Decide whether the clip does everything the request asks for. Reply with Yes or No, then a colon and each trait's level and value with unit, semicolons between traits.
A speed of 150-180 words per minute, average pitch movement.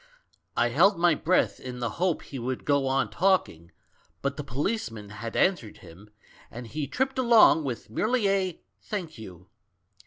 No: average, 160 wpm; wide, 8.2 semitones